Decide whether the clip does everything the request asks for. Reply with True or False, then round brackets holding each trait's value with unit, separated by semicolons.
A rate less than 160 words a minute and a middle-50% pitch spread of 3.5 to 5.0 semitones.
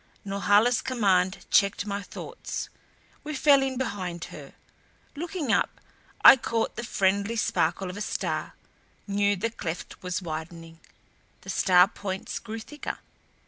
True (135 wpm; 4.1 semitones)